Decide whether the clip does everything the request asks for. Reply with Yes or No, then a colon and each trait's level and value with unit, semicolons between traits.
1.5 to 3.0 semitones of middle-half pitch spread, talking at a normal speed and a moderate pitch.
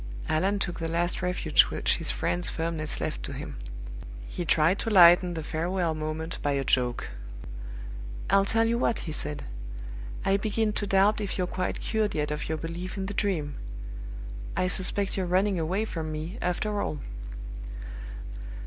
No: average, 4.0 semitones; average, 165 wpm; medium, 180 Hz